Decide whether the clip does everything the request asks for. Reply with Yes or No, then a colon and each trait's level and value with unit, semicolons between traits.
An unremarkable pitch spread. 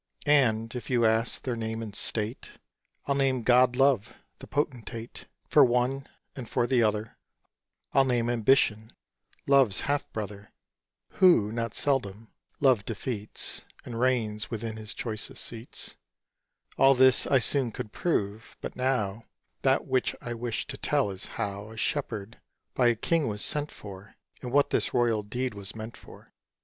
Yes: average, 3.3 semitones